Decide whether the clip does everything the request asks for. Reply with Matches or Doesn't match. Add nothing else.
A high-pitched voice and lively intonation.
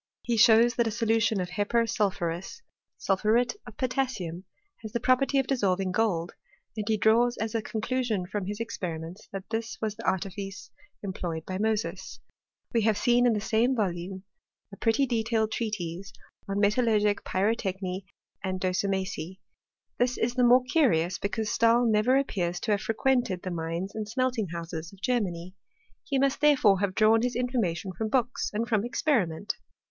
Doesn't match